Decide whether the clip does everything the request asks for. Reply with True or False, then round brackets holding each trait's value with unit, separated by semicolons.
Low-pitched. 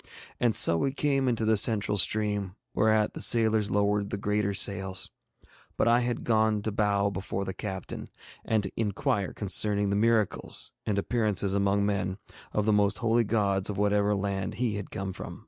True (105 Hz)